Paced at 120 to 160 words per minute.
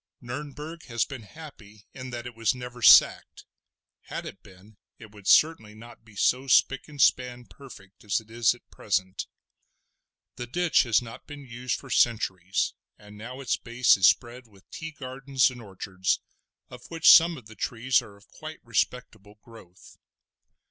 No: average, 170 wpm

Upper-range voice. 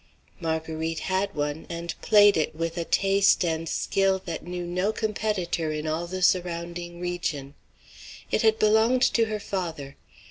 No: medium, 175 Hz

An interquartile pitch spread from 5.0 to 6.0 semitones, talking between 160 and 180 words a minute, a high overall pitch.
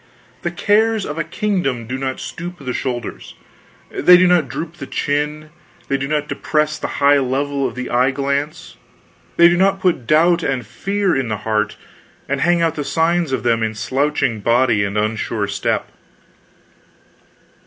No: average, 5.3 semitones; average, 170 wpm; medium, 140 Hz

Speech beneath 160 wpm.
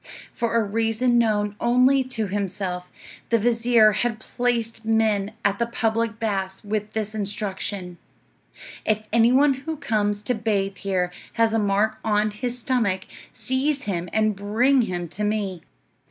Yes: average, 150 wpm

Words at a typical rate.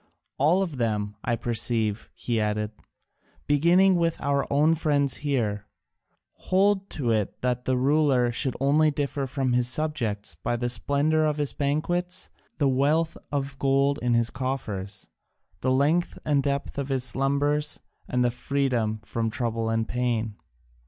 Yes: average, 150 wpm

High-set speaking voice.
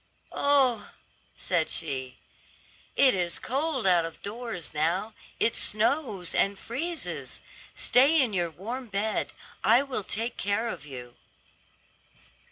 Yes: high, 215 Hz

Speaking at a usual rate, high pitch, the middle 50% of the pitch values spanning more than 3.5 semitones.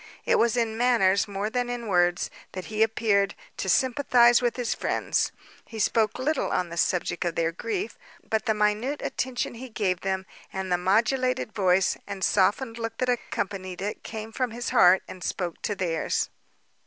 Yes: average, 180 wpm; high, 215 Hz; average, 4.2 semitones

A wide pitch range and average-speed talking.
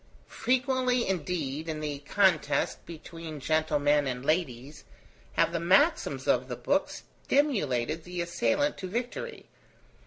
No: wide, 7.3 semitones; slow, 120 wpm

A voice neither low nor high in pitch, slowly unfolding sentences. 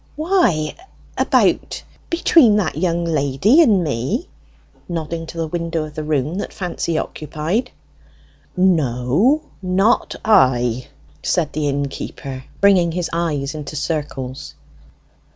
Yes: medium, 165 Hz; slow, 115 wpm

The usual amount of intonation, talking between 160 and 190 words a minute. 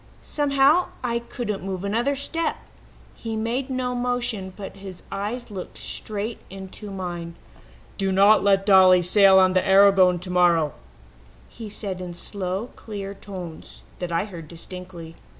No: average, 3.6 semitones; average, 140 wpm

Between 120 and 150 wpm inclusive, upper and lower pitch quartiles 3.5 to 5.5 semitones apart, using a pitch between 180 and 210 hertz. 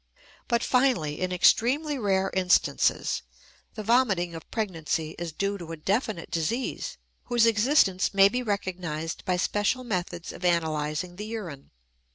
Yes: average, 140 wpm; average, 5.2 semitones; high, 190 Hz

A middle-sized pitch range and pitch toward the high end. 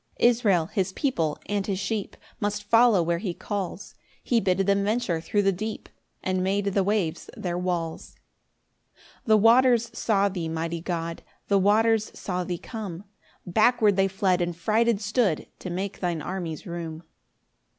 Yes: average, 3.6 semitones; high, 195 Hz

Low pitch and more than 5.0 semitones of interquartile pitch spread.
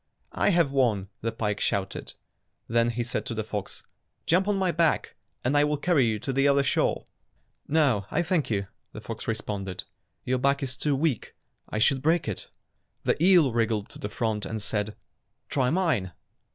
Yes: low, 125 Hz; wide, 5.6 semitones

